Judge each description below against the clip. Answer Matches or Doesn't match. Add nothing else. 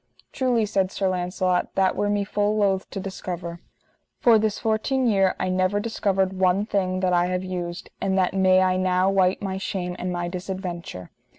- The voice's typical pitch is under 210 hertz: Matches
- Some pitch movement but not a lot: Doesn't match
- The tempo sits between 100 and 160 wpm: Doesn't match